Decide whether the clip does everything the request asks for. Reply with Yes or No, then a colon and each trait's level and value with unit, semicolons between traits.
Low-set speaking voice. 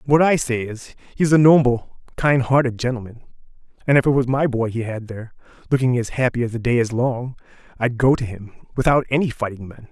Yes: low, 125 Hz